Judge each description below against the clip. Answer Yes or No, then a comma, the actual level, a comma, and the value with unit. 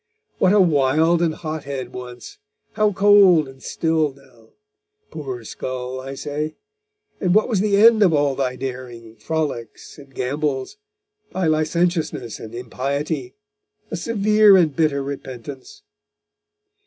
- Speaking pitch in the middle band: Yes, medium, 150 Hz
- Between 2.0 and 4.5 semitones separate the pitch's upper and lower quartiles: No, average, 5.2 semitones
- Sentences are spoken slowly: Yes, slow, 130 wpm